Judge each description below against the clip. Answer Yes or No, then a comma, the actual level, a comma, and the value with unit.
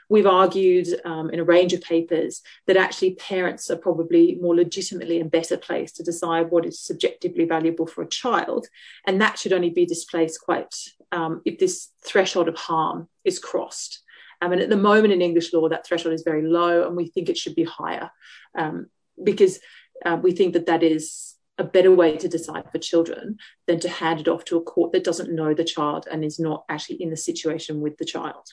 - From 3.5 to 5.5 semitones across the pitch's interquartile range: No, average, 2.8 semitones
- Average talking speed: No, fast, 210 wpm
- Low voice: No, medium, 175 Hz